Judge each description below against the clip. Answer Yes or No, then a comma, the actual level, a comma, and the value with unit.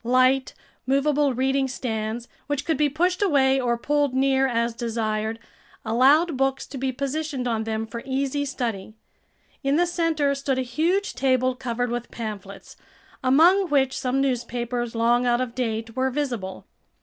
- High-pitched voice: Yes, very high, 260 Hz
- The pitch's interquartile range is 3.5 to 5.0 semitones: No, average, 2.9 semitones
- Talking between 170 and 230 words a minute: No, average, 155 wpm